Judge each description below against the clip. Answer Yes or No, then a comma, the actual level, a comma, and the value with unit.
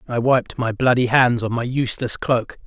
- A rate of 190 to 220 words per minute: Yes, average, 200 wpm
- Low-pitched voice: Yes, low, 120 Hz